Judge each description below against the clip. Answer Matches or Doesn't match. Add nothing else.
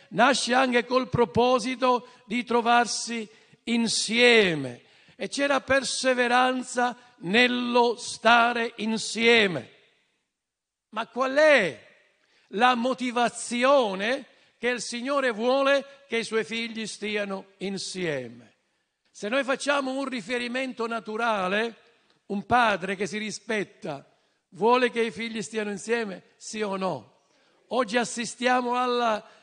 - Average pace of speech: Doesn't match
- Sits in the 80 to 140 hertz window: Doesn't match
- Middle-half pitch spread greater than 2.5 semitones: Matches